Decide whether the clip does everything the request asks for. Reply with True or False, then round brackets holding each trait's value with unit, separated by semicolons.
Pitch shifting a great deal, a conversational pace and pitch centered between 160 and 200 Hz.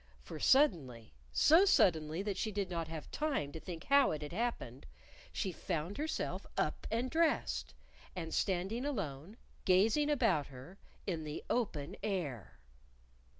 True (7.5 semitones; 145 wpm; 185 Hz)